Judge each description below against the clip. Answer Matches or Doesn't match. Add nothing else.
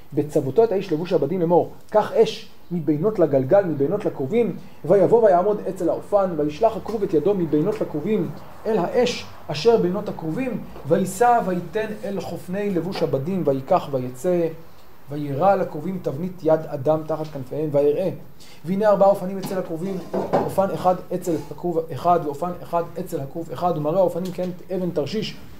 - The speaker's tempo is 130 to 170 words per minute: Matches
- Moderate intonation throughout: Matches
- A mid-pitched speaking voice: Matches